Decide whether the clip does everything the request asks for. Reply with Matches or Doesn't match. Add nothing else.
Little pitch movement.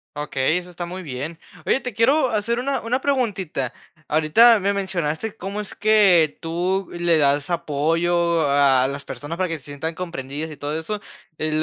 Doesn't match